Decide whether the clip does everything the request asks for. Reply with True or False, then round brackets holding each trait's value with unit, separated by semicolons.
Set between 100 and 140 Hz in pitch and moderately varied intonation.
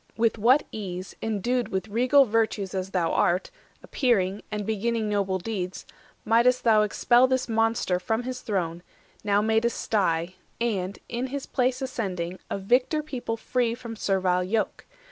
False (220 Hz; 4.0 semitones)